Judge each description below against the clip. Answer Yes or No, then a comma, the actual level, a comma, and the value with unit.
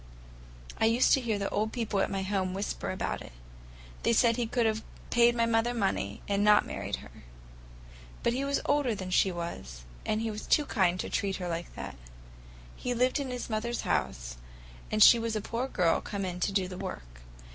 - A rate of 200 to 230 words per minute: Yes, fast, 205 wpm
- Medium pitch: No, high, 210 Hz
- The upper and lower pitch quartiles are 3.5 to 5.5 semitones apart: Yes, average, 4.1 semitones